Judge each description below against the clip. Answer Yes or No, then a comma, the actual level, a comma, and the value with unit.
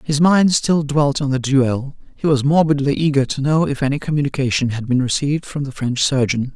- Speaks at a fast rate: Yes, fast, 210 wpm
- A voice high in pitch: No, medium, 140 Hz